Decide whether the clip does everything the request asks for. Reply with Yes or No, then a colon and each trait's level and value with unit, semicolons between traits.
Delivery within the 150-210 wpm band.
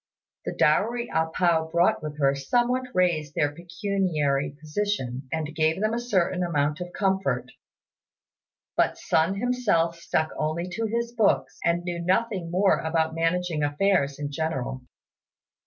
No: average, 140 wpm